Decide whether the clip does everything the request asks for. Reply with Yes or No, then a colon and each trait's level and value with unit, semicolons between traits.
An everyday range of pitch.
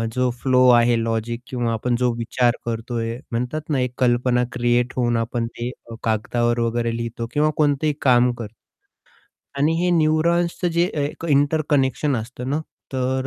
Yes: average, 3.2 semitones